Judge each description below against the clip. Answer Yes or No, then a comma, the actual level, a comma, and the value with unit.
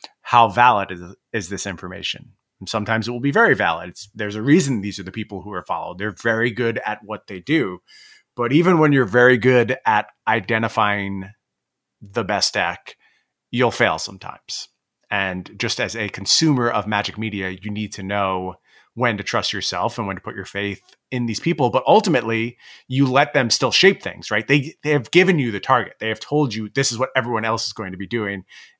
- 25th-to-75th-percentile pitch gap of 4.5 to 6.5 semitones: No, average, 4.1 semitones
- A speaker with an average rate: No, fast, 210 wpm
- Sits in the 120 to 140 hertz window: No, low, 110 Hz